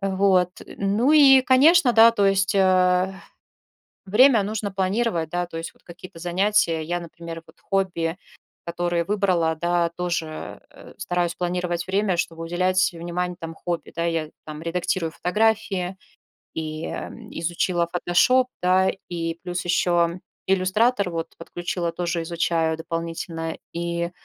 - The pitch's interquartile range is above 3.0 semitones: No, narrow, 2.5 semitones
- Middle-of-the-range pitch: Yes, medium, 175 Hz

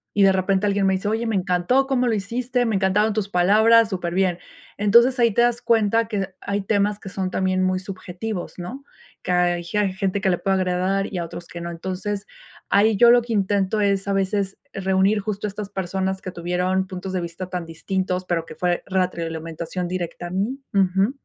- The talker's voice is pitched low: No, high, 195 Hz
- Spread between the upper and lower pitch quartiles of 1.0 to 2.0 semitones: No, narrow, 2.4 semitones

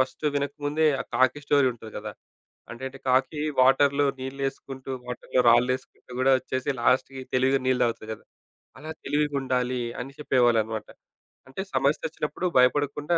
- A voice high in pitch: No, low, 130 Hz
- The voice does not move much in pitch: Yes, narrow, 2.0 semitones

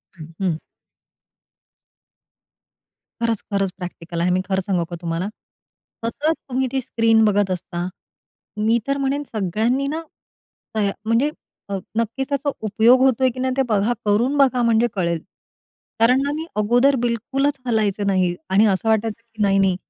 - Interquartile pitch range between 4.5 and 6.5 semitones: Yes, average, 4.8 semitones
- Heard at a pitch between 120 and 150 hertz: No, high, 220 Hz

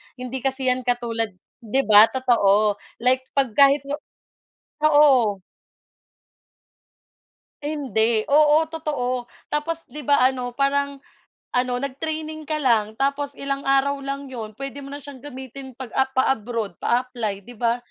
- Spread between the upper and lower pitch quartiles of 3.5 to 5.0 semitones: No, average, 2.9 semitones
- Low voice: No, very high, 260 Hz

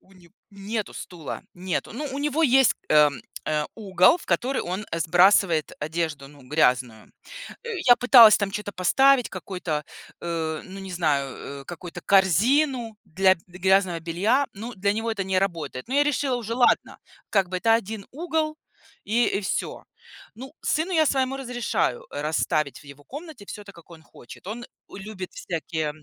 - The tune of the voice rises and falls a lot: Yes, wide, 6.4 semitones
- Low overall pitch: No, high, 195 Hz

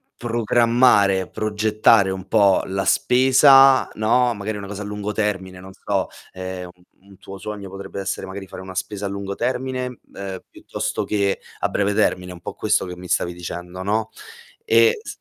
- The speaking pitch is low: Yes, low, 100 Hz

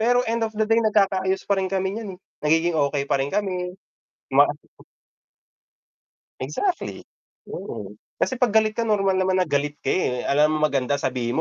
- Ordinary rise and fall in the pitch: No, wide, 6.3 semitones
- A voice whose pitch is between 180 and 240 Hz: Yes, high, 190 Hz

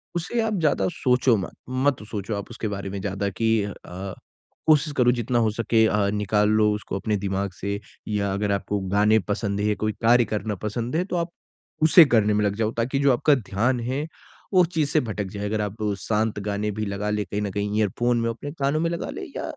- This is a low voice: Yes, low, 110 Hz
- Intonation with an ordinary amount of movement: Yes, average, 3.5 semitones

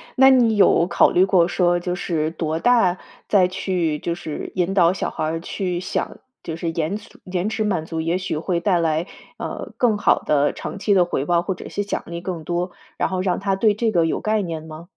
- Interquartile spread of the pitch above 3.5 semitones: No, average, 2.9 semitones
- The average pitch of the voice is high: No, medium, 180 Hz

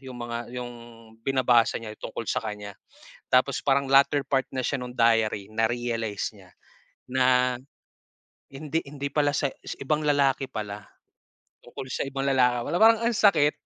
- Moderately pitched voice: No, low, 125 Hz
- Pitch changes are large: No, average, 3.3 semitones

